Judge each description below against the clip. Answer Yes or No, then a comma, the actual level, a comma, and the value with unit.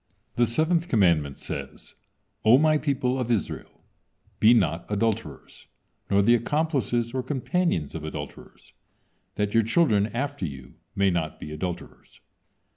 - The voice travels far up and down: Yes, wide, 6.9 semitones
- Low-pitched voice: Yes, low, 115 Hz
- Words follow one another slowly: Yes, slow, 130 wpm